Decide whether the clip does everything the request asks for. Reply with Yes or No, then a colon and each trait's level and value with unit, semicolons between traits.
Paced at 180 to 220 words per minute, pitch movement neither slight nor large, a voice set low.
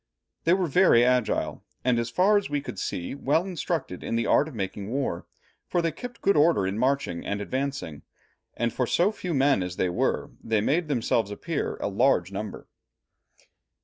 No: average, 185 wpm; wide, 7.9 semitones; low, 130 Hz